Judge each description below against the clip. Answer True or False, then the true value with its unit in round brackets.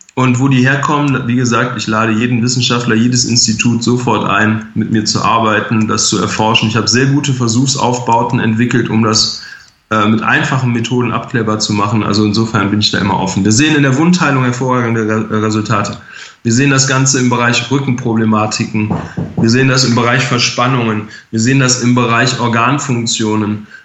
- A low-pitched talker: True (120 Hz)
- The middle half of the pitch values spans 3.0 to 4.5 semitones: False (2.5 semitones)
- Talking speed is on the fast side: False (175 wpm)